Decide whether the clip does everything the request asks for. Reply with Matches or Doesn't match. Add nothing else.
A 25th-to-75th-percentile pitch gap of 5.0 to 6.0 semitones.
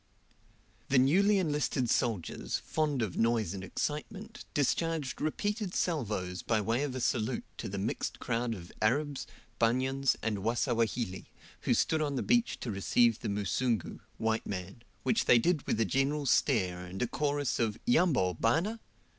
Matches